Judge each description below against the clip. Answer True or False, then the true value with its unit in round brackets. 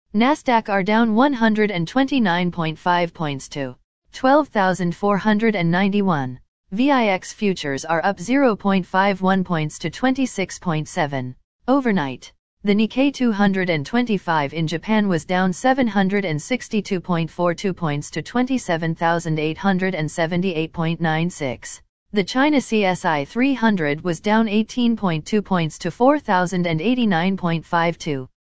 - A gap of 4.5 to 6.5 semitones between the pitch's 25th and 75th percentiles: True (4.9 semitones)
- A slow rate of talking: True (80 wpm)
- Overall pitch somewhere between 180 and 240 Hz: True (185 Hz)